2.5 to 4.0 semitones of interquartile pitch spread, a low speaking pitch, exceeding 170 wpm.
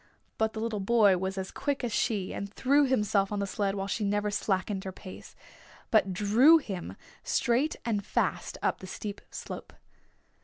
No: average, 2.9 semitones; high, 205 Hz; average, 180 wpm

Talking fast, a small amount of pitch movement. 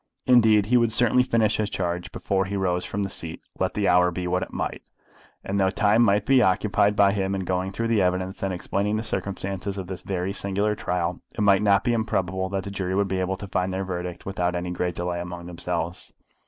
Yes: fast, 230 wpm; narrow, 2.1 semitones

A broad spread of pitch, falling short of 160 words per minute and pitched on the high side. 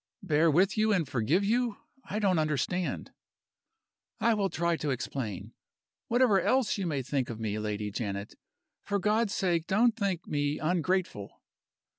No: wide, 6.8 semitones; average, 150 wpm; medium, 170 Hz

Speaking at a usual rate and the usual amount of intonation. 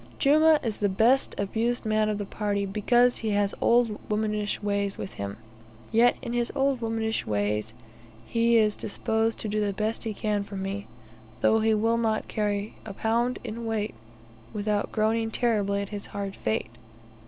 No: average, 175 wpm; narrow, 2.2 semitones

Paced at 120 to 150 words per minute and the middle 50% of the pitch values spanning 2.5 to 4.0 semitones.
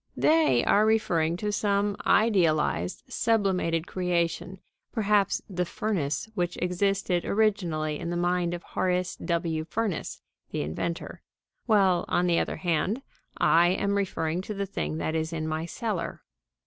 Yes: average, 140 wpm; average, 3.4 semitones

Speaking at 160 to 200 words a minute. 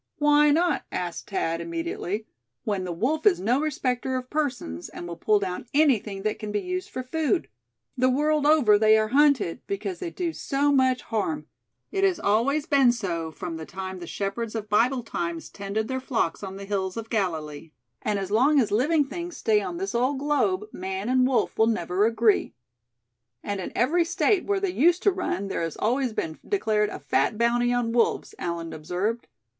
Yes: average, 195 wpm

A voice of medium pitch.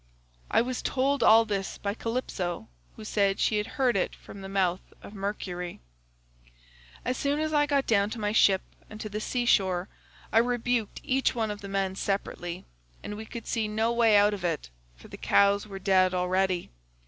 No: high, 205 Hz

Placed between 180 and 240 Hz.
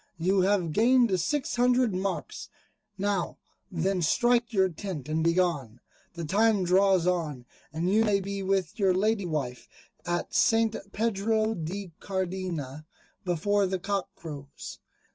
Yes: high, 190 Hz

